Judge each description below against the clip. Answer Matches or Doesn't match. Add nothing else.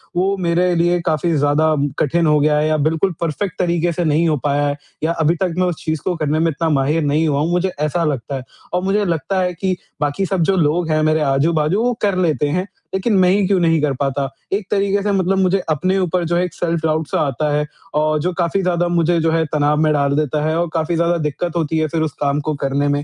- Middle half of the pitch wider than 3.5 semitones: Doesn't match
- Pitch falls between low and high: Matches